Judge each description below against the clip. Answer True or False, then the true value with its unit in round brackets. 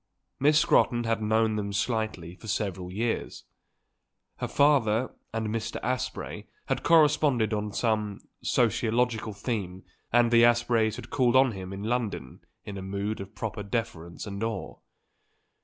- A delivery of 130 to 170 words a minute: True (140 wpm)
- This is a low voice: True (110 Hz)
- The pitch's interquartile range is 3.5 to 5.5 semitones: False (3.0 semitones)